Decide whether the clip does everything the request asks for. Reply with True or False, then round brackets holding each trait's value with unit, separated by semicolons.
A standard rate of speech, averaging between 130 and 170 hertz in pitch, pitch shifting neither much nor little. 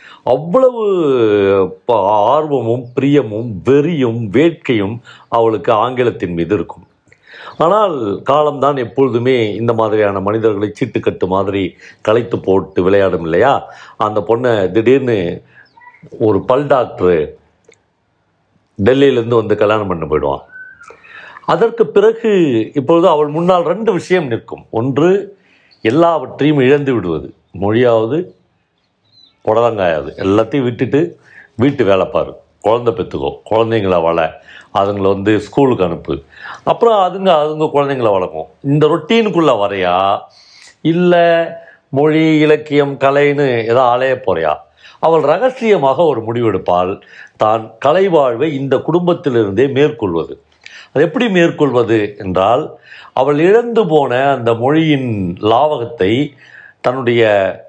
False (100 wpm; 135 Hz; 6.8 semitones)